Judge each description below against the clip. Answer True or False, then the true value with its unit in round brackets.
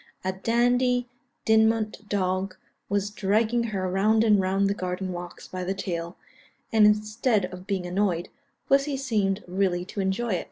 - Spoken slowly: False (155 wpm)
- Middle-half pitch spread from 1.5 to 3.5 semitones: True (2.9 semitones)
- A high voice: True (200 Hz)